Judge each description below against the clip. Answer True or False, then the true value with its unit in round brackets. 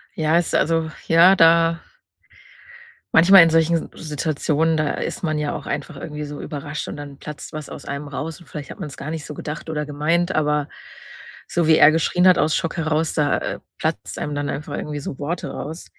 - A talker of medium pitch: True (155 Hz)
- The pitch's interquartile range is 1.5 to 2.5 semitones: True (1.8 semitones)